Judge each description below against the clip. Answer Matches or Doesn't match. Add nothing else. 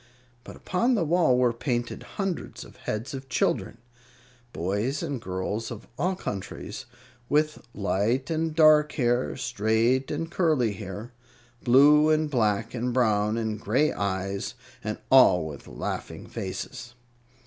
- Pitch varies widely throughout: Matches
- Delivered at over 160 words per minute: Doesn't match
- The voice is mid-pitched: Doesn't match